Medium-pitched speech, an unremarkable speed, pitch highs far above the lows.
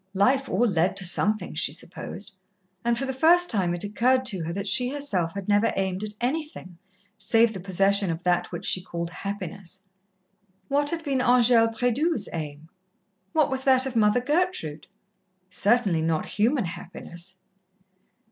No: high, 210 Hz; average, 160 wpm; wide, 6.0 semitones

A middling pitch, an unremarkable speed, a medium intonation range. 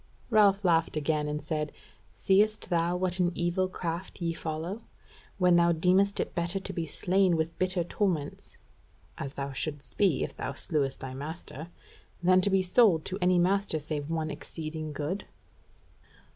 Yes: medium, 170 Hz; average, 160 wpm; average, 3.2 semitones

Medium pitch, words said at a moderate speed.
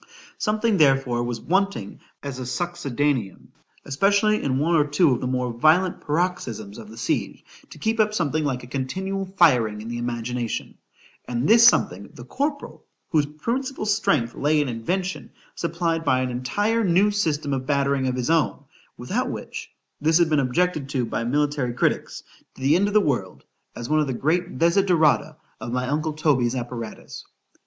Yes: medium, 145 Hz; average, 170 wpm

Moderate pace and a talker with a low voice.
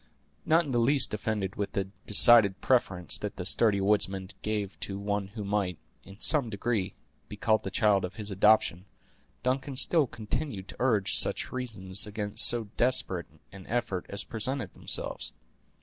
Yes: average, 165 wpm; low, 105 Hz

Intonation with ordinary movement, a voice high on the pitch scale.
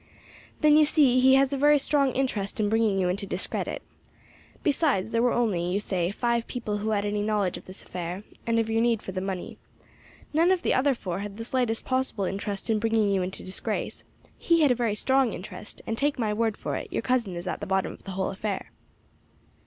Yes: average, 4.8 semitones; high, 220 Hz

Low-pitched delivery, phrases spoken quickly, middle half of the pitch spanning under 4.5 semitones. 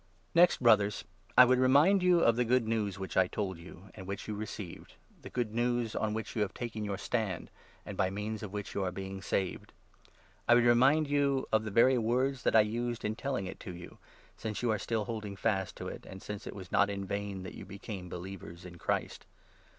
Yes: low, 105 Hz; fast, 235 wpm; average, 3.8 semitones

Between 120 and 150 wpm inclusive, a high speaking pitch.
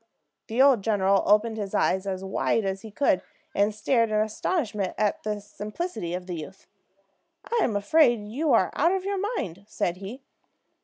No: average, 170 wpm; high, 210 Hz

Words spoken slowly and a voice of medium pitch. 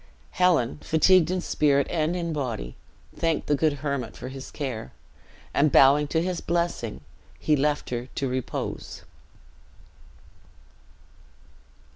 Yes: slow, 120 wpm; medium, 150 Hz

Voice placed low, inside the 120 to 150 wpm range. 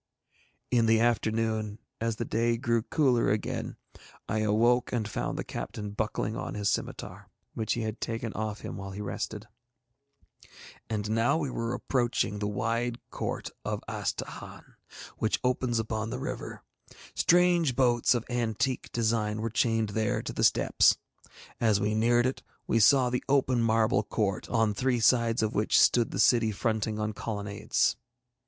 No: low, 115 Hz; average, 160 wpm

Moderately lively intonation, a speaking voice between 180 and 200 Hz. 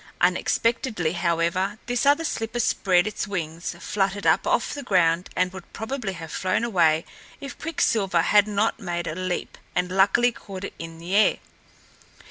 Yes: average, 4.2 semitones; high, 190 Hz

